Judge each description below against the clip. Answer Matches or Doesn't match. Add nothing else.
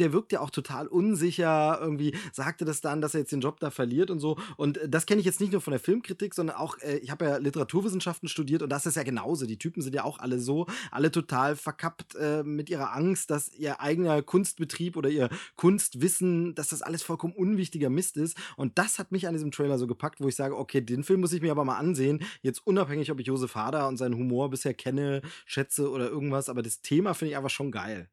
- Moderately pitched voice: Matches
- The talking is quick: Matches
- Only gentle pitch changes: Doesn't match